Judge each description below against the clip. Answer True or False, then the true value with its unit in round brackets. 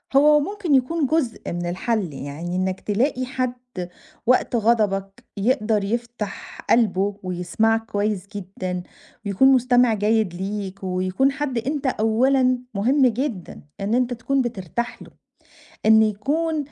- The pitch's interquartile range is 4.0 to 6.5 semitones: True (4.7 semitones)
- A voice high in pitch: True (225 Hz)